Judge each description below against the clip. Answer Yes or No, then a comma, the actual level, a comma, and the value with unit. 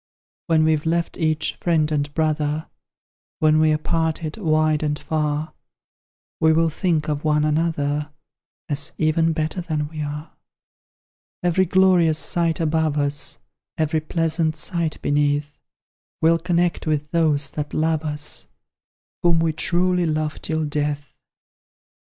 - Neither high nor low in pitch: Yes, medium, 155 Hz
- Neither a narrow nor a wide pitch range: No, narrow, 1.5 semitones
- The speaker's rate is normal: No, slow, 125 wpm